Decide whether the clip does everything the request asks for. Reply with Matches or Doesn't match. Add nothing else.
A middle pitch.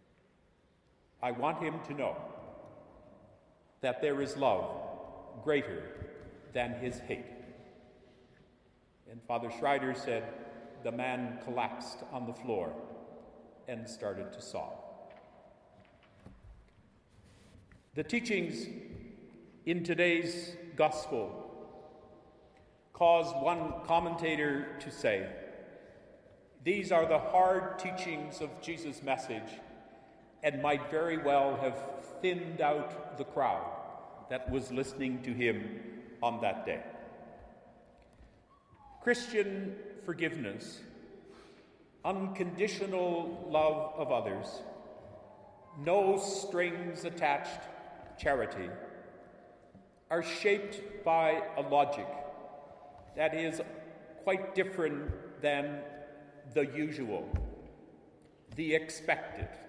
Matches